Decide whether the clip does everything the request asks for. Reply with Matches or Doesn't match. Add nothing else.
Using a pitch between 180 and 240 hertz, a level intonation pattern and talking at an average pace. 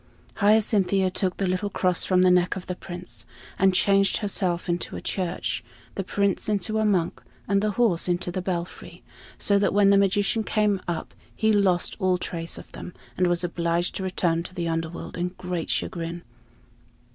Matches